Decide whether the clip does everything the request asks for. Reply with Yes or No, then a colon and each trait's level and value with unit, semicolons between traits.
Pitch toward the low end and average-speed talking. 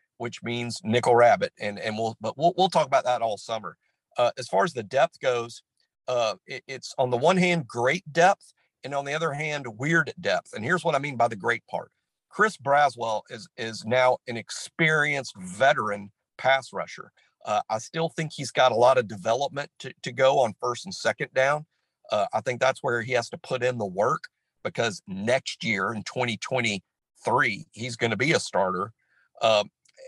Yes: low, 130 Hz; average, 195 wpm